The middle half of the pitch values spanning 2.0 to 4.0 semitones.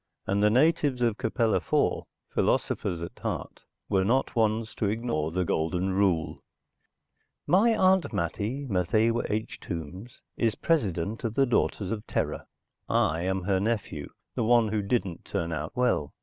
No: average, 4.7 semitones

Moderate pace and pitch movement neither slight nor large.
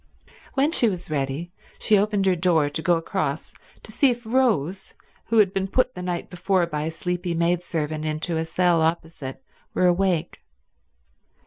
Yes: average, 170 wpm; average, 3.2 semitones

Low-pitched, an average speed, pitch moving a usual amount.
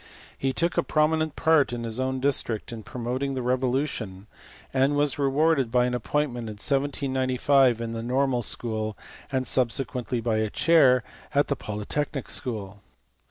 Yes: low, 130 Hz; average, 160 wpm; average, 3.2 semitones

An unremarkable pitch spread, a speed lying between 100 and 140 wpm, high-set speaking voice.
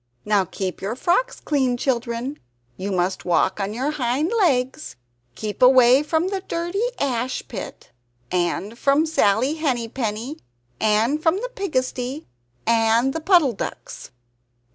No: wide, 5.8 semitones; slow, 135 wpm; very high, 255 Hz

